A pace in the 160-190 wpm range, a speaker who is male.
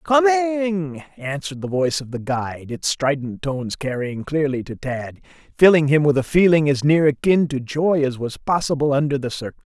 Yes: average, 185 wpm; male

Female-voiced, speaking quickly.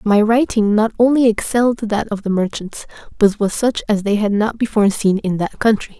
Yes: female; fast, 210 wpm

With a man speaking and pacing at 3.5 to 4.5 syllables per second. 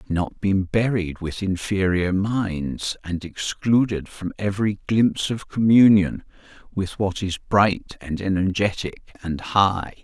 Yes: male; 4.0 syllables/s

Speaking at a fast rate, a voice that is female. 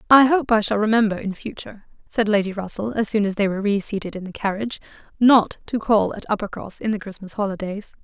Yes: fast, 210 wpm; female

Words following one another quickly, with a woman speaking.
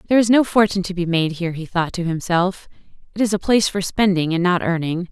Yes: fast, 245 wpm; female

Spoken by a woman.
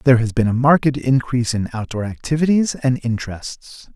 No: male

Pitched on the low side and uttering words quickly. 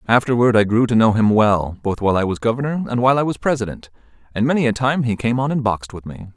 Yes: low, 115 Hz; fast, 265 wpm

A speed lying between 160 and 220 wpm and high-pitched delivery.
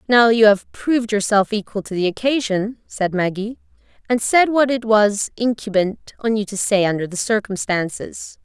Yes: average, 170 wpm; high, 215 Hz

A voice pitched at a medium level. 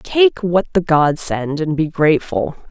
Yes: medium, 160 Hz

